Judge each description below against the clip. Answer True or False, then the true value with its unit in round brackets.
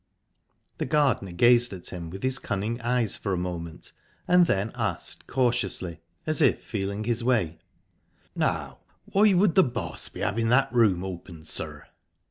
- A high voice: False (115 Hz)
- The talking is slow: False (155 wpm)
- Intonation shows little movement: False (5.5 semitones)